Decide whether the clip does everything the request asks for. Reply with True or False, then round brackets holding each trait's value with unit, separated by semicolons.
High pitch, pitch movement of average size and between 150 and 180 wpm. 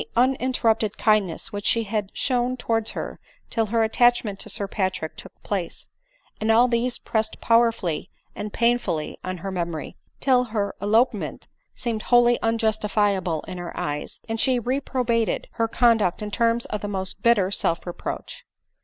True (220 Hz; 3.1 semitones; 155 wpm)